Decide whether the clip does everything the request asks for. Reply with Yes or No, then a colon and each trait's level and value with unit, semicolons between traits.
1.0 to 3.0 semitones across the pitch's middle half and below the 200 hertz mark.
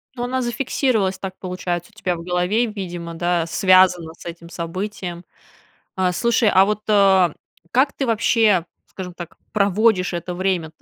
No: average, 3.4 semitones; medium, 185 Hz